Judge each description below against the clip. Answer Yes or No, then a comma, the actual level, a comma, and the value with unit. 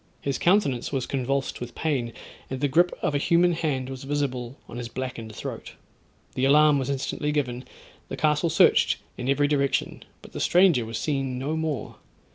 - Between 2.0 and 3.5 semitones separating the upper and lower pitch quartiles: Yes, average, 2.8 semitones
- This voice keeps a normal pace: Yes, average, 180 wpm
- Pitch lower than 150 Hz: Yes, medium, 140 Hz